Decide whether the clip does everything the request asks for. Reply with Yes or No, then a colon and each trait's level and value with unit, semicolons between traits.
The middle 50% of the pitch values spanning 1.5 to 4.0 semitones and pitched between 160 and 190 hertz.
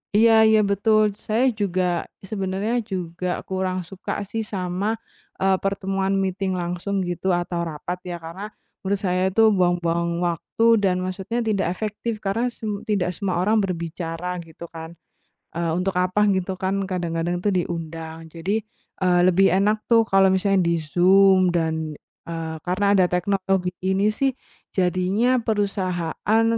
Yes: narrow, 2.4 semitones; medium, 185 Hz